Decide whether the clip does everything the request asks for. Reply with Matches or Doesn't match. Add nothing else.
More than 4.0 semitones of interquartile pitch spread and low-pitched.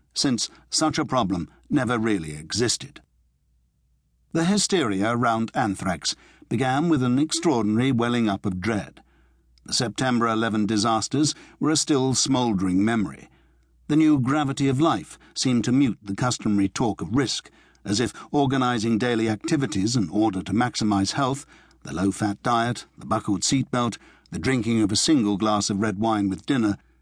Matches